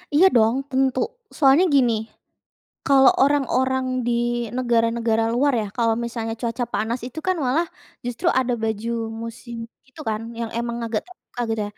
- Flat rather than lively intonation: Yes, narrow, 2.3 semitones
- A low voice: No, high, 240 Hz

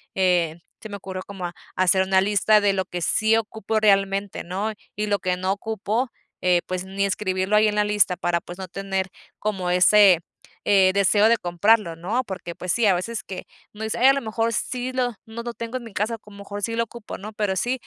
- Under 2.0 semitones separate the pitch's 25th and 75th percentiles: No, average, 2.8 semitones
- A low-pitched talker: No, high, 200 Hz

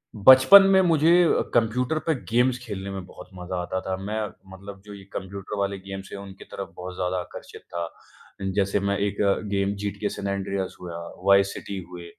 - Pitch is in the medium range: No, low, 100 Hz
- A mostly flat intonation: Yes, narrow, 1.8 semitones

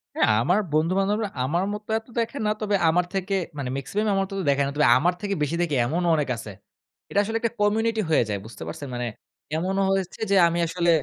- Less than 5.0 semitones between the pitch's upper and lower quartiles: No, wide, 5.6 semitones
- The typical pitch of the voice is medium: Yes, medium, 180 Hz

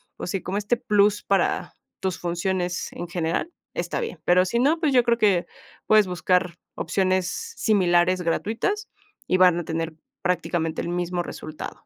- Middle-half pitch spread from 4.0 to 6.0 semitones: No, average, 3.2 semitones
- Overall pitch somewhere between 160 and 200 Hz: Yes, medium, 185 Hz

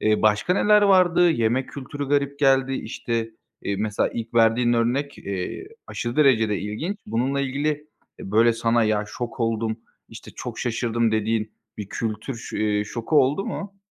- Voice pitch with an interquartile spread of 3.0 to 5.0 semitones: Yes, average, 4.3 semitones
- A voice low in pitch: Yes, low, 120 Hz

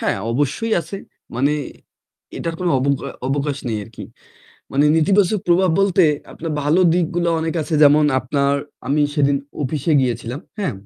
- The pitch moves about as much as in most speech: Yes, average, 3.8 semitones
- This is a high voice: No, medium, 150 Hz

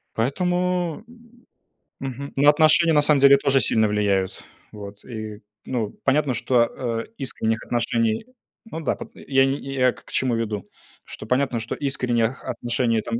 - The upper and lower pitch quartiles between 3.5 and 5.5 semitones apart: Yes, average, 3.9 semitones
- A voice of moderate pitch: No, low, 130 Hz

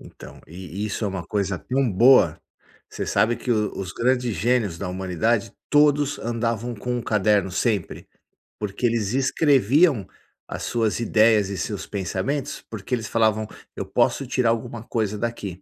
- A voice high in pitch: No, low, 110 Hz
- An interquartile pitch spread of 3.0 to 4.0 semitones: Yes, average, 3.6 semitones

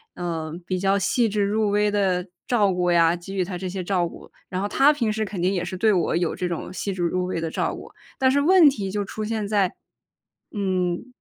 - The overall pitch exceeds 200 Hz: No, high, 195 Hz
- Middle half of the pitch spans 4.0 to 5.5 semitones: No, average, 2.9 semitones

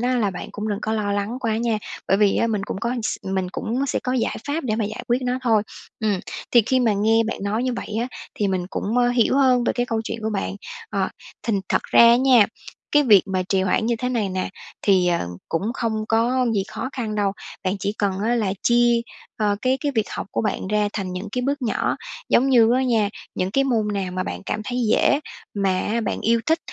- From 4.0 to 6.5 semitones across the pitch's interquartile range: No, average, 3.3 semitones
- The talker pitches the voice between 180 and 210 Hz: No, high, 220 Hz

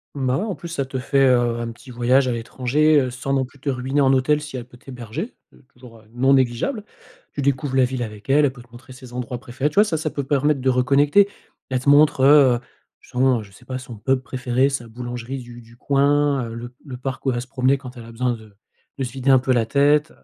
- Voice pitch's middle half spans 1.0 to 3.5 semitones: Yes, narrow, 2.4 semitones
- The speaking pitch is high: No, low, 130 Hz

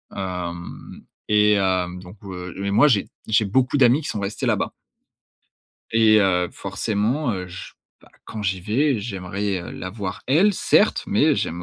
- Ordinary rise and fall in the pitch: Yes, average, 3.4 semitones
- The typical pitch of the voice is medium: No, low, 100 Hz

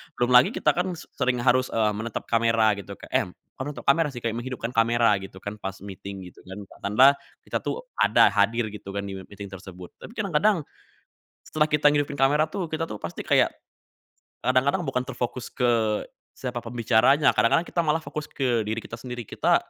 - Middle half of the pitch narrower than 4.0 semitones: No, average, 5.0 semitones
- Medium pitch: No, low, 125 Hz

